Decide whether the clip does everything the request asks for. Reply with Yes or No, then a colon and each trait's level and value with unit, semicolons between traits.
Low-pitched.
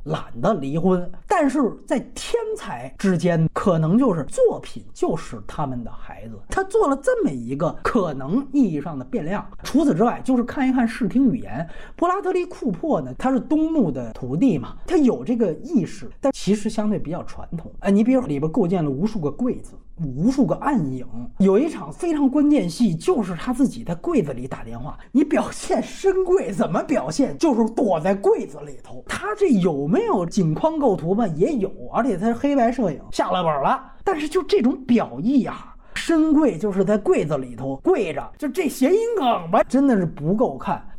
No: high, 235 Hz